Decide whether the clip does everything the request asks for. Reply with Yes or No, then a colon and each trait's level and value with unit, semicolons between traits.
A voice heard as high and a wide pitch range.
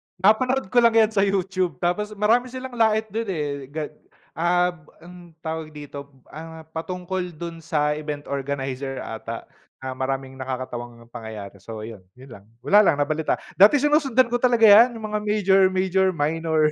No: medium, 170 Hz; wide, 6.8 semitones